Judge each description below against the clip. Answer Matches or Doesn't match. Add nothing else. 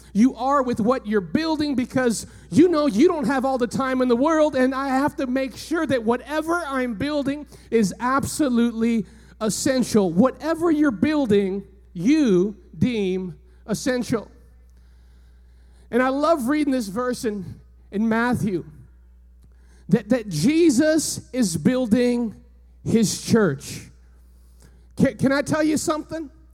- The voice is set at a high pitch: Matches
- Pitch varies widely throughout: Matches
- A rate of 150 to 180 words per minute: Doesn't match